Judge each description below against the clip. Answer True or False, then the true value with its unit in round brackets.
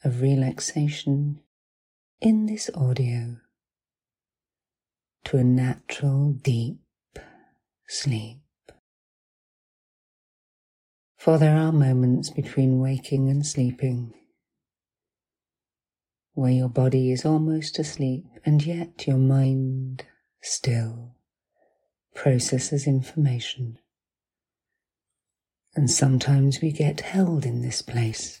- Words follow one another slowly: True (80 wpm)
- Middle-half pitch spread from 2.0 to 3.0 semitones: True (2.7 semitones)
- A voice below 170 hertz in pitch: True (135 Hz)